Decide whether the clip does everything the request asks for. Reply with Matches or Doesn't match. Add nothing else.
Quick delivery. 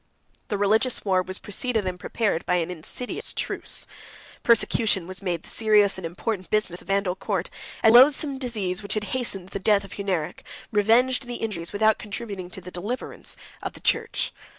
Doesn't match